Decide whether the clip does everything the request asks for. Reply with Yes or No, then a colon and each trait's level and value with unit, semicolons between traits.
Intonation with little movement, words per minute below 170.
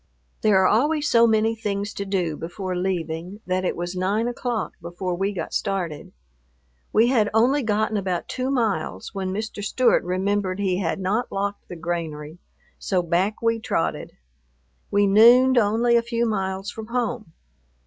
No: average, 3.7 semitones; average, 160 wpm